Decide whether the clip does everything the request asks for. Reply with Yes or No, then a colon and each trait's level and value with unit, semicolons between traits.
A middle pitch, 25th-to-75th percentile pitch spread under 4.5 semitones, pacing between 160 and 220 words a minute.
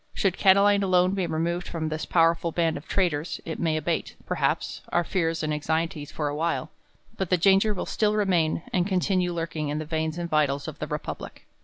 Yes: medium, 170 Hz; average, 2.8 semitones; average, 200 wpm